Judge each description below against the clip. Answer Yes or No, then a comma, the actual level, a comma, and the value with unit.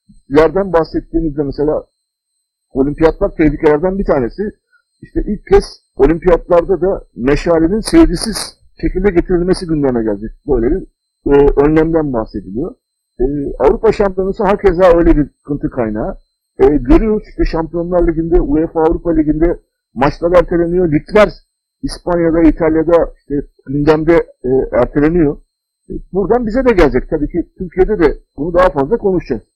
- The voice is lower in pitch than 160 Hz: No, medium, 165 Hz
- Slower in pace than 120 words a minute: No, average, 125 wpm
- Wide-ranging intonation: No, average, 4.2 semitones